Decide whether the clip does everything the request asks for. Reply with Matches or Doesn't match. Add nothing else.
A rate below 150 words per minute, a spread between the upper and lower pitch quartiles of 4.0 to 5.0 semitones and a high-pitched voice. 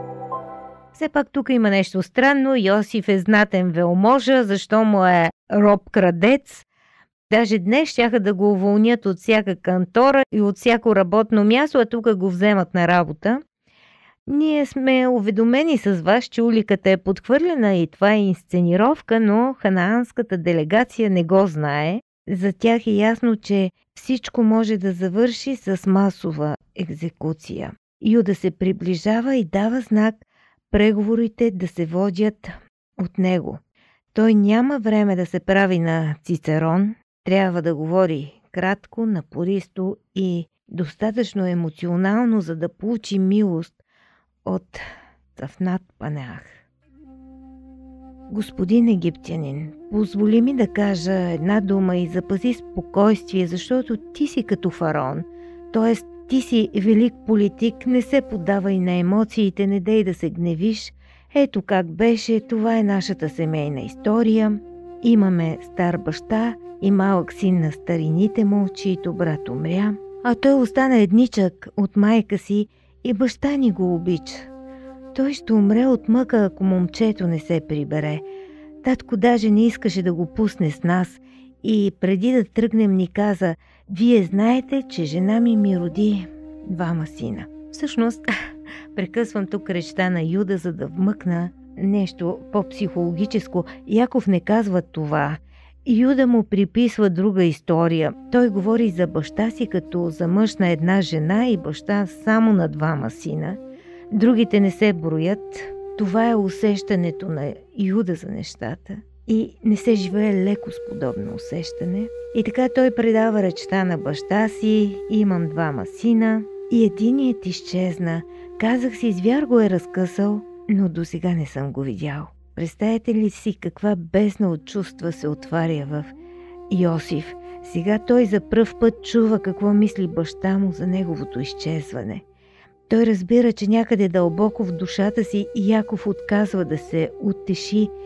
Matches